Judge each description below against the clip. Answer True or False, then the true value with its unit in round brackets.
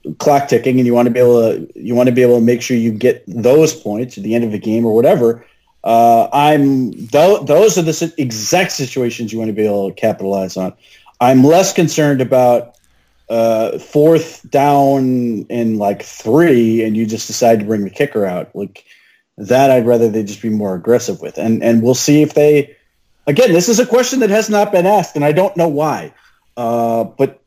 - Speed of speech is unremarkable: False (210 wpm)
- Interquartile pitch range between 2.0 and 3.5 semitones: False (4.6 semitones)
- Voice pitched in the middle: False (120 Hz)